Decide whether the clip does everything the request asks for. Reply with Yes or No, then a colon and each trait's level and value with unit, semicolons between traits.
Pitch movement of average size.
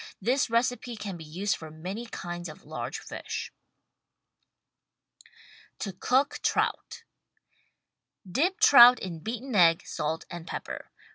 No: wide, 6.1 semitones